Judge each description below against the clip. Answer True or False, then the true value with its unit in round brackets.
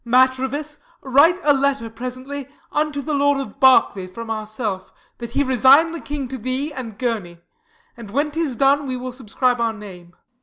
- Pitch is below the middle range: False (260 Hz)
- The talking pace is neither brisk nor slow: True (175 wpm)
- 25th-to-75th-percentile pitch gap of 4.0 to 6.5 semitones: False (3.6 semitones)